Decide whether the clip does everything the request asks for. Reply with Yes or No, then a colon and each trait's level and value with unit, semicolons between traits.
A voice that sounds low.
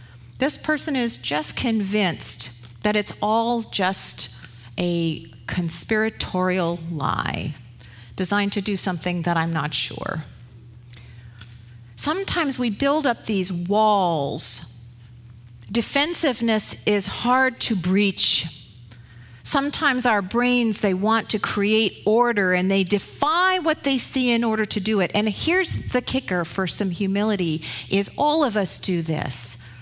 No: high, 190 Hz